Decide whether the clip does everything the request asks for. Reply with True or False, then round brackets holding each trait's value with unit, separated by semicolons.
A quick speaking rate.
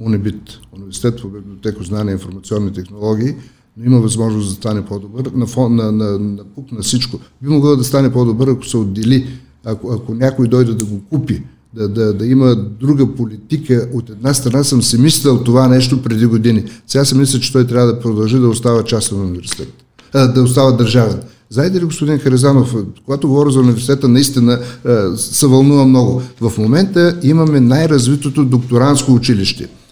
True (175 wpm)